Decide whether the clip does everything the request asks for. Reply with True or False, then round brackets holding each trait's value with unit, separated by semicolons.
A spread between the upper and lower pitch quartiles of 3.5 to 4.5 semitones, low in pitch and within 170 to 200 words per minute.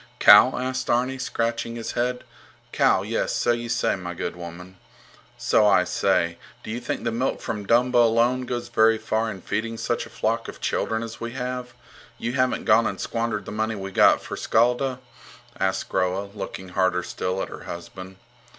True (4.0 semitones; 115 Hz; 185 wpm)